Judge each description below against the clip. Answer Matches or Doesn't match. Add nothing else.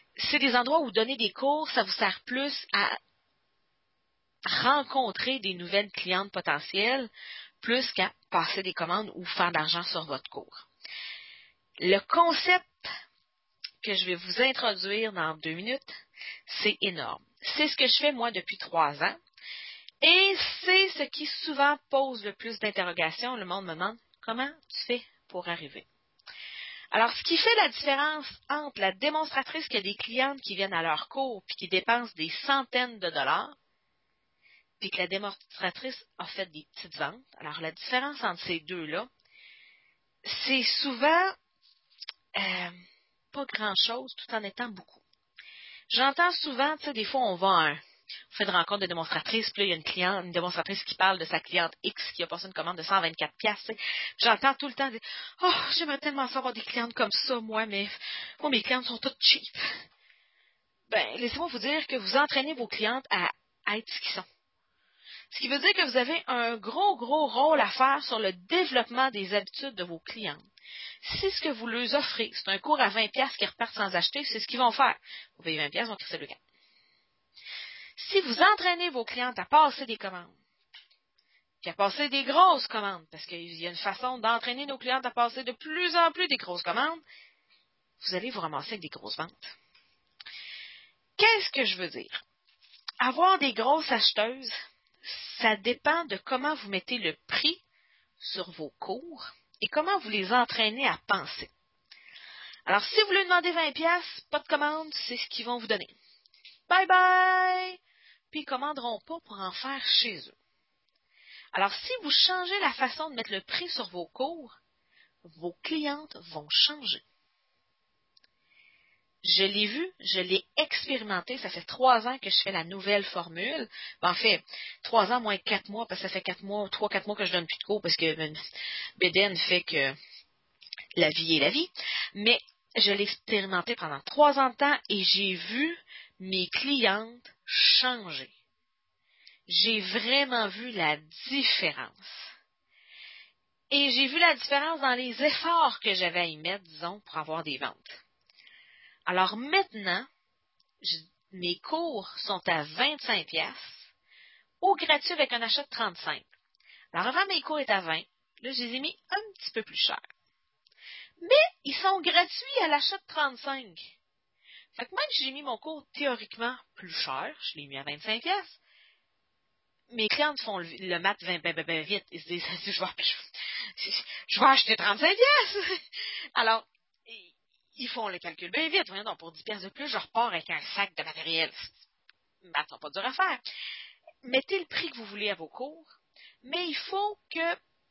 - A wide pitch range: Matches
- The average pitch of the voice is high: Matches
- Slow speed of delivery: Doesn't match